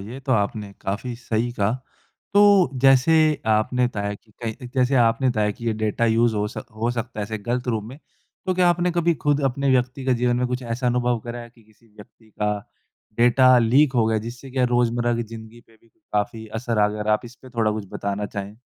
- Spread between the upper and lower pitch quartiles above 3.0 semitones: No, average, 2.7 semitones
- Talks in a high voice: No, low, 120 Hz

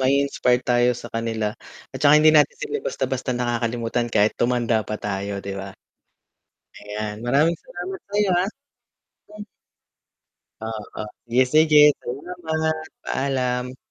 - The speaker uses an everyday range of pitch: Yes, average, 5.0 semitones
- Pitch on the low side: Yes, low, 125 Hz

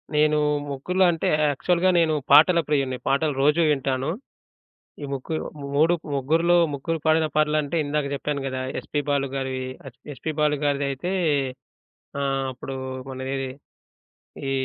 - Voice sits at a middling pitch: Yes, medium, 145 Hz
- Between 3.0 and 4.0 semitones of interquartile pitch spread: No, narrow, 2.6 semitones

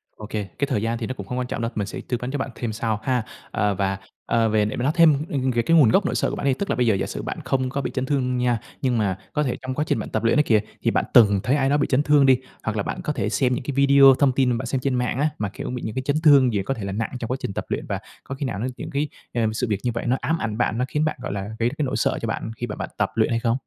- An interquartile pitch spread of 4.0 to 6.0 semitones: No, average, 3.6 semitones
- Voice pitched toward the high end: No, low, 125 Hz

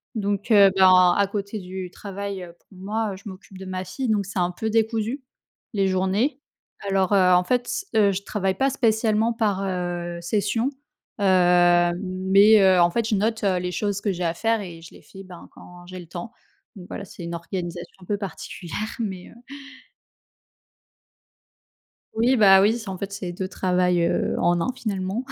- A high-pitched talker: Yes, high, 195 Hz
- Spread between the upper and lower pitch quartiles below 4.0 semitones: Yes, average, 2.8 semitones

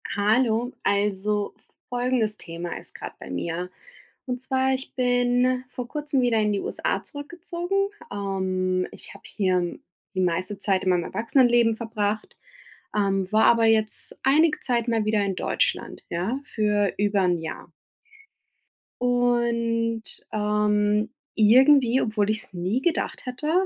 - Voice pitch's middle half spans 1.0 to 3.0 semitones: No, average, 3.6 semitones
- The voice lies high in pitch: Yes, high, 220 Hz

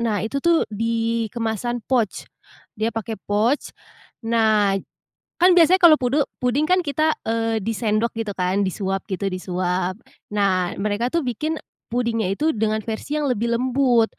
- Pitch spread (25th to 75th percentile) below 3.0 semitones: No, average, 3.7 semitones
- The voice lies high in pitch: Yes, high, 225 Hz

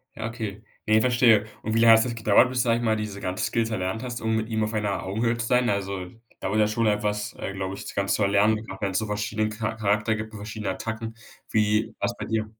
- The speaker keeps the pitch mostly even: Yes, narrow, 1.5 semitones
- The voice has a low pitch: Yes, low, 110 Hz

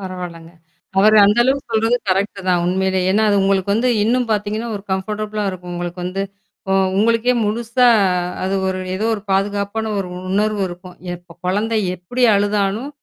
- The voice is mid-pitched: No, high, 200 Hz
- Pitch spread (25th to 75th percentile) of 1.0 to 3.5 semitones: Yes, average, 2.8 semitones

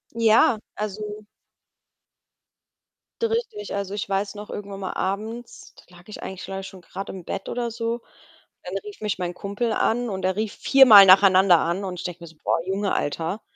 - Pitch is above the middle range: Yes, high, 200 Hz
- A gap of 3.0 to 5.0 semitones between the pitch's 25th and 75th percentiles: No, narrow, 2.6 semitones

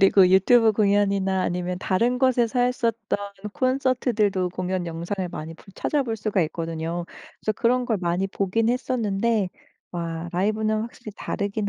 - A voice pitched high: Yes, high, 205 Hz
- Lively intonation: No, average, 4.2 semitones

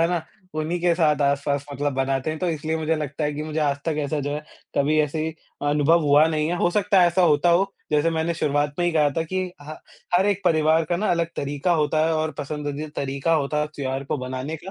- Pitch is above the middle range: No, medium, 155 Hz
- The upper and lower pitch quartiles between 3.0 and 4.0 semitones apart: No, narrow, 2.4 semitones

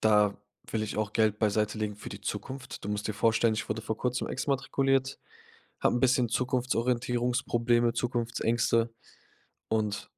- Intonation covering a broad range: No, narrow, 2.4 semitones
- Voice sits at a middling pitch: No, low, 115 Hz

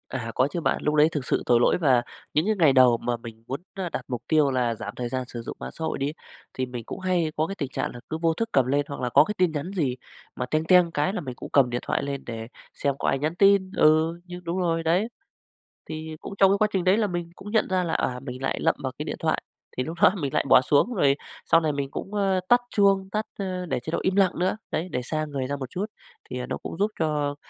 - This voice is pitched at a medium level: Yes, medium, 155 Hz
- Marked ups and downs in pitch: Yes, wide, 5.7 semitones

